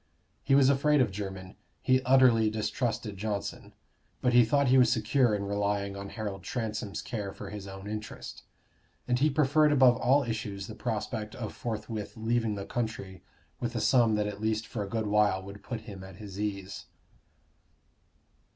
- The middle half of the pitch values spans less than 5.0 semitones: Yes, average, 3.3 semitones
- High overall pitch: No, low, 110 Hz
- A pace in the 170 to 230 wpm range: Yes, average, 175 wpm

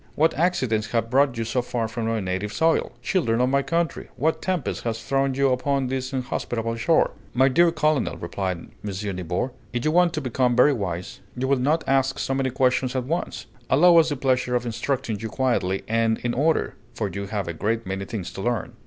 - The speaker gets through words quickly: Yes, fast, 210 wpm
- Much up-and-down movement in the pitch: No, average, 3.7 semitones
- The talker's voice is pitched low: Yes, low, 125 Hz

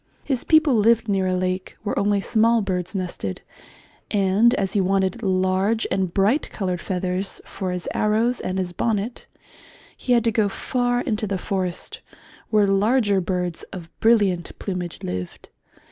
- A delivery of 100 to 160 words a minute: Yes, average, 155 wpm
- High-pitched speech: Yes, high, 195 Hz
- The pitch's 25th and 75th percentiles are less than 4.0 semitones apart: Yes, average, 3.4 semitones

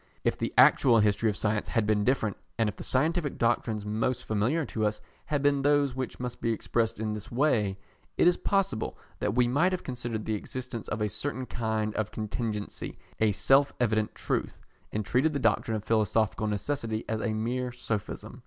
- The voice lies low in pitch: Yes, low, 115 Hz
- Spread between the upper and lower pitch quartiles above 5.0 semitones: No, average, 3.2 semitones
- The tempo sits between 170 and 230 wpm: Yes, average, 190 wpm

